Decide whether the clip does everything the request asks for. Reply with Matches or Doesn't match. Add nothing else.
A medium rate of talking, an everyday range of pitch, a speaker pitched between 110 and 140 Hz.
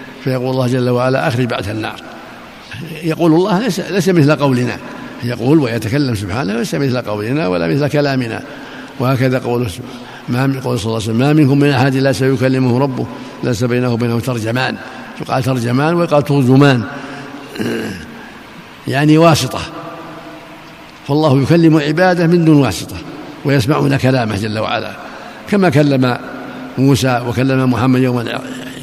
Matches